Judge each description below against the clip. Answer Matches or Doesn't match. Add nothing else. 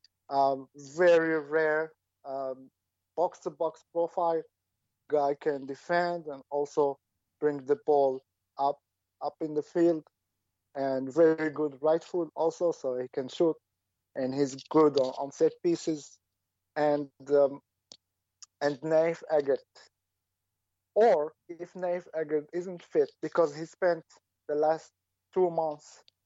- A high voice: Doesn't match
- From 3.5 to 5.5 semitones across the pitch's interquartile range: Matches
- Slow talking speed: Matches